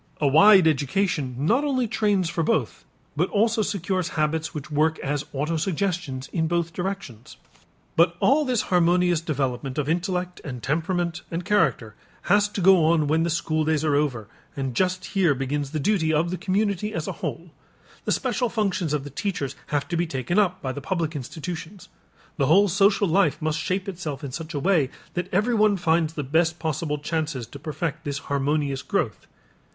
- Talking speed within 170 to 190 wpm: Yes, average, 180 wpm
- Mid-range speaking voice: Yes, medium, 165 Hz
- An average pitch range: Yes, average, 4.2 semitones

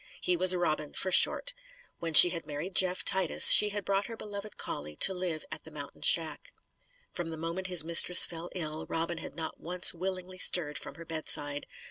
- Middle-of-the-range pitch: Yes, medium, 175 Hz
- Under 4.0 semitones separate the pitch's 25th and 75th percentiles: Yes, average, 2.8 semitones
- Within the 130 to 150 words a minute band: No, average, 195 wpm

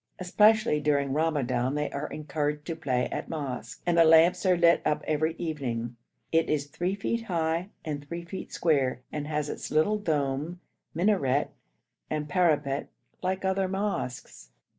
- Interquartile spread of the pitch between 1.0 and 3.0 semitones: No, average, 3.6 semitones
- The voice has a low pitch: No, medium, 155 Hz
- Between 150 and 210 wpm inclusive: Yes, average, 155 wpm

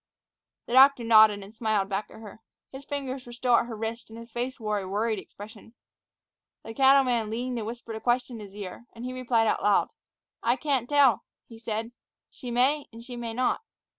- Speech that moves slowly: No, fast, 205 wpm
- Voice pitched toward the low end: No, high, 235 Hz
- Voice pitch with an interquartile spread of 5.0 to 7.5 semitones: No, narrow, 2.5 semitones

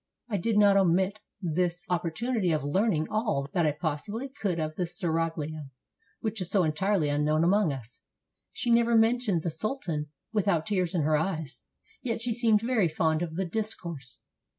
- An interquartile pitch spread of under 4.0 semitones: No, average, 5.3 semitones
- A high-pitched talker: No, medium, 180 Hz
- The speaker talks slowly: No, average, 175 wpm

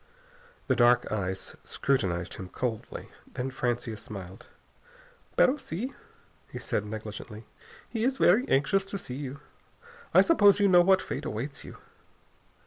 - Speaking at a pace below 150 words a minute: Yes, slow, 135 wpm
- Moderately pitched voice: No, low, 130 Hz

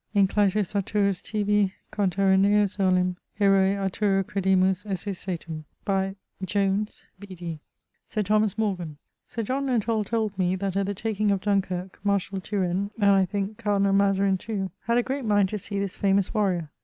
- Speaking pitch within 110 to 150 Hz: No, high, 195 Hz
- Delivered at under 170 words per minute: Yes, average, 155 wpm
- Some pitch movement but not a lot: No, narrow, 1.5 semitones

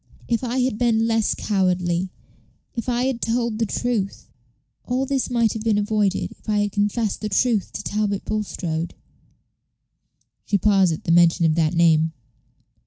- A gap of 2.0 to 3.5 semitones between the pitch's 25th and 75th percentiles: No, average, 4.1 semitones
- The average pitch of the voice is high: Yes, high, 210 Hz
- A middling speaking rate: Yes, average, 165 wpm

